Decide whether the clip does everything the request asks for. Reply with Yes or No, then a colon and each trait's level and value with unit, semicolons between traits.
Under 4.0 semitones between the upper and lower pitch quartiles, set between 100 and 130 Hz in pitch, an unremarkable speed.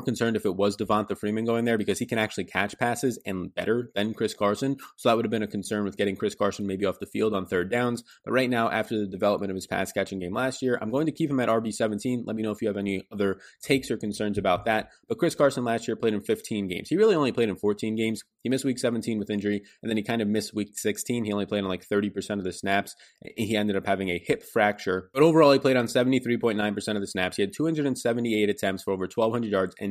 No: average, 2.9 semitones; low, 110 Hz; fast, 275 wpm